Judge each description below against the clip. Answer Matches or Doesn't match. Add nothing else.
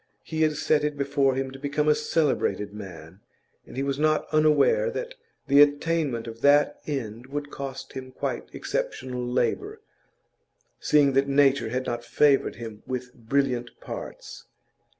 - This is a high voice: Doesn't match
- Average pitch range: Matches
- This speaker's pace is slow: Doesn't match